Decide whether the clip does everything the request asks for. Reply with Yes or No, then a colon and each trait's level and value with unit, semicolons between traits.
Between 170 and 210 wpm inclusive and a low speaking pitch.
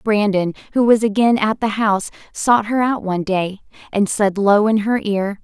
No: average, 200 wpm; high, 210 Hz